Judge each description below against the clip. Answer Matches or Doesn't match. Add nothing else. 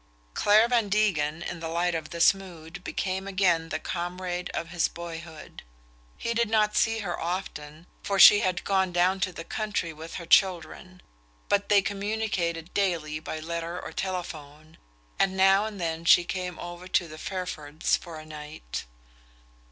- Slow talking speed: Doesn't match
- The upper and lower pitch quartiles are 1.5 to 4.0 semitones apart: Matches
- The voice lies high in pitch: Doesn't match